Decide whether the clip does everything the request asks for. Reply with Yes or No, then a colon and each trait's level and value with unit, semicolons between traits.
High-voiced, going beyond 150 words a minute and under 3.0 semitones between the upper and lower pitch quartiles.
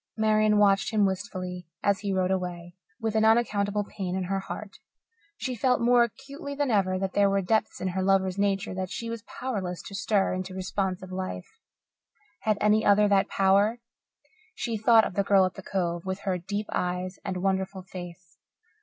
Yes: high, 195 Hz; average, 185 wpm; narrow, 2.4 semitones